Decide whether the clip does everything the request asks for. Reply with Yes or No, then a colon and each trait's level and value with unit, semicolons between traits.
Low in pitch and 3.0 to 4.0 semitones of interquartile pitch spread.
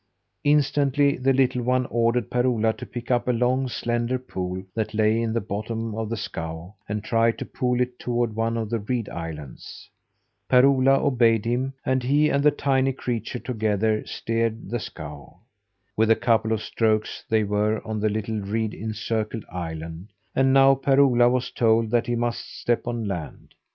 No: low, 115 Hz; narrow, 2.6 semitones